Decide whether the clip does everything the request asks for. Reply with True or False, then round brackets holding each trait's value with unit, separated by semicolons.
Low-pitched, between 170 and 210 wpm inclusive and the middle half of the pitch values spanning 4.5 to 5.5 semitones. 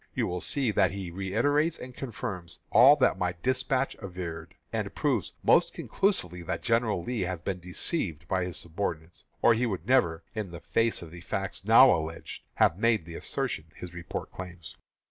True (95 Hz; 180 wpm; 5.2 semitones)